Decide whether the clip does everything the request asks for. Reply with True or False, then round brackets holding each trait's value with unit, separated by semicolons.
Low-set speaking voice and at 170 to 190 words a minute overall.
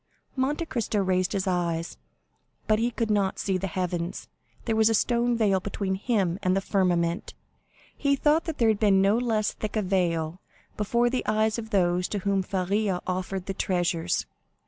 False (195 Hz; 180 wpm)